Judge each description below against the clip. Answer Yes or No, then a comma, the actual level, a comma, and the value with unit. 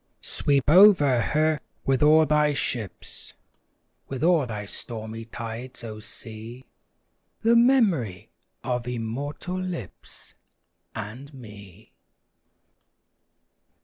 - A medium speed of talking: No, slow, 90 wpm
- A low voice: Yes, low, 130 Hz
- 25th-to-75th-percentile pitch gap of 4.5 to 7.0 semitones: Yes, wide, 5.4 semitones